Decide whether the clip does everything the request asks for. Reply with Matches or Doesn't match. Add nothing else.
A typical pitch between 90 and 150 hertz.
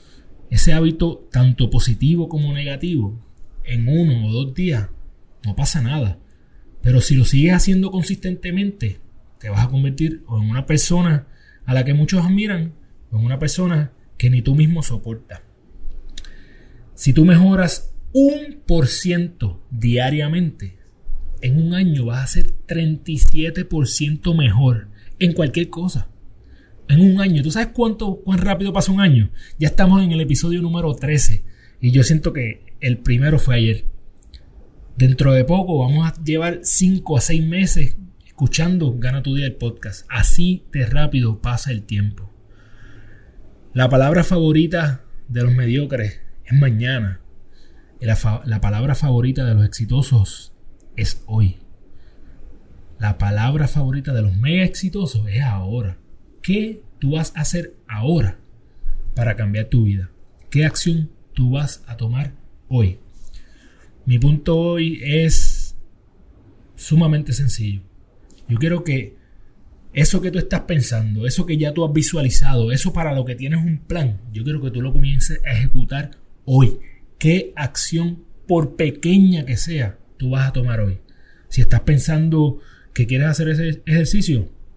Matches